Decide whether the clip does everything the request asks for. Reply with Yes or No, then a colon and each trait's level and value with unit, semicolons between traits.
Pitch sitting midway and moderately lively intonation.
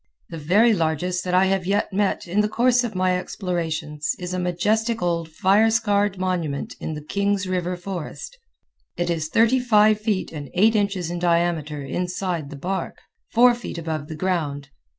Yes: medium, 180 Hz; average, 3.7 semitones